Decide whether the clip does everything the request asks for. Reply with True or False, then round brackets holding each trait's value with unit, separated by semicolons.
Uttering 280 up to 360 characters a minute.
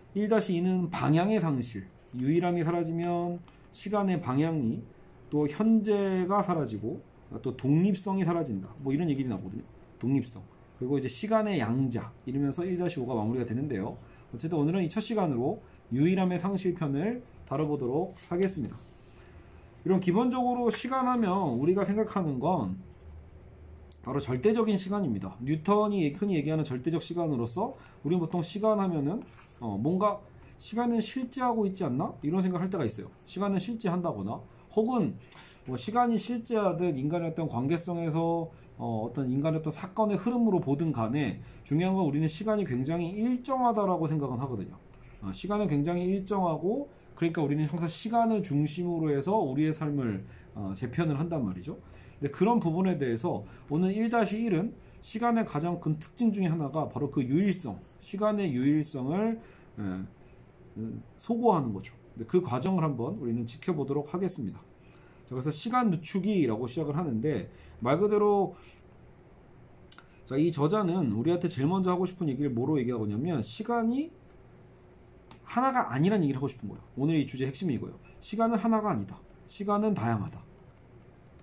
True (340 characters per minute)